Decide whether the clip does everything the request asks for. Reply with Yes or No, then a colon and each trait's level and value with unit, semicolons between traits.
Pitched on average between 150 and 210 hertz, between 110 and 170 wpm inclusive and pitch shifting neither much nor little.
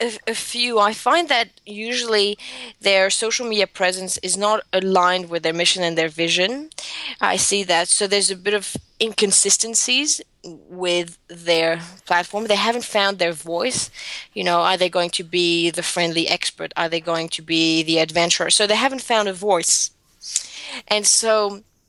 Yes: high, 190 Hz; average, 165 wpm; average, 3.9 semitones